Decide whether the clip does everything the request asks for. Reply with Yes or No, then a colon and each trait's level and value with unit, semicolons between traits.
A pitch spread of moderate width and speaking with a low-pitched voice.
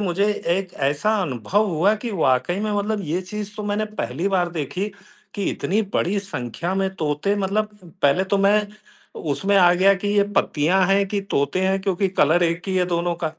No: average, 3.2 semitones; high, 190 Hz